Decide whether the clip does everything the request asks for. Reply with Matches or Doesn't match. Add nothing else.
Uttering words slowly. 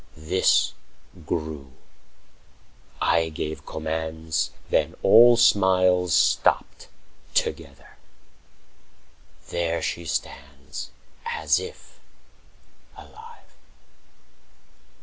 Matches